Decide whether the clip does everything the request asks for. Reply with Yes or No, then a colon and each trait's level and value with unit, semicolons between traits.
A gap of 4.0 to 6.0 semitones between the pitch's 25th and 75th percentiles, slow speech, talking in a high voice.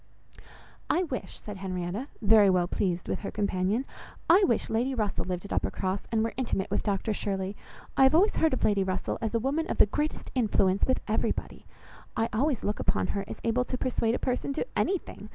No: average, 4.9 semitones; fast, 205 wpm; high, 220 Hz